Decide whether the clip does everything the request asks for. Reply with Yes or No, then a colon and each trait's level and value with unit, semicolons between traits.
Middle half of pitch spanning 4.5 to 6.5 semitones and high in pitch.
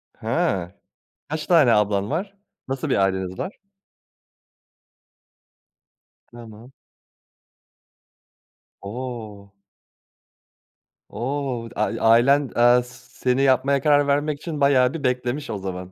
No: average, 4.8 semitones; low, 125 Hz